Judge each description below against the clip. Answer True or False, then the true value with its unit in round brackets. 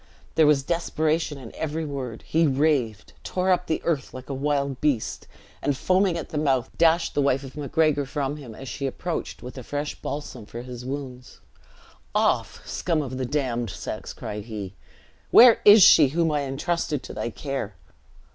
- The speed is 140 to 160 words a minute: False (180 wpm)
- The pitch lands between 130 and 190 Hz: True (140 Hz)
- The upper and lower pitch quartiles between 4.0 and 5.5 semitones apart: False (3.6 semitones)